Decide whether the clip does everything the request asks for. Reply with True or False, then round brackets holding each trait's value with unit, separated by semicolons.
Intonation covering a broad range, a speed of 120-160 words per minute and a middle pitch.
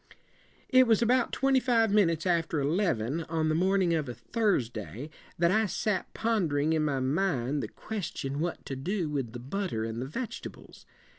False (6.9 semitones; 195 wpm; 165 Hz)